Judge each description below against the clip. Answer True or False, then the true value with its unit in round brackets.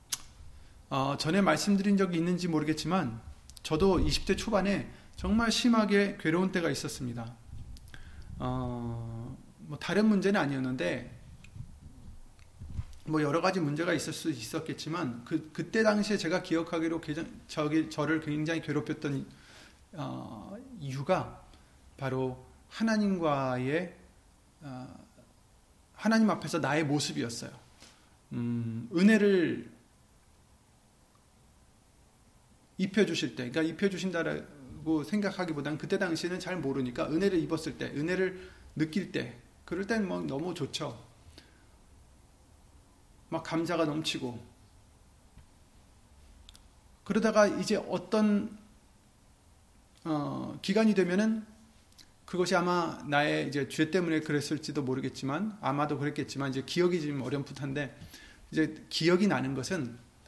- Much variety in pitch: True (6.1 semitones)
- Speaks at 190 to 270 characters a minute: True (250 characters per minute)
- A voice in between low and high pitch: True (155 Hz)